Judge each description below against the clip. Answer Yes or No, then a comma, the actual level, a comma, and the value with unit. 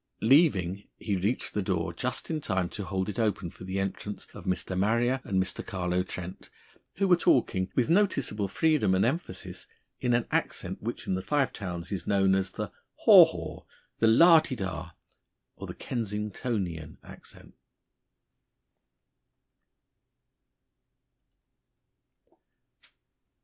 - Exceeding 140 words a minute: No, slow, 135 wpm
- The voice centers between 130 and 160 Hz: No, low, 100 Hz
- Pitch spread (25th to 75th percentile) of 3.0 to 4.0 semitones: No, average, 4.8 semitones